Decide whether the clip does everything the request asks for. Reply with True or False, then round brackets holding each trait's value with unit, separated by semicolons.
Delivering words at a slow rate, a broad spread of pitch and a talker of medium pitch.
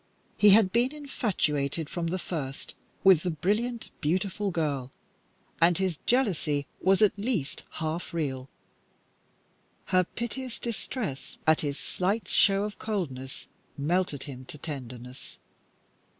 True (120 wpm; 6.4 semitones; 175 Hz)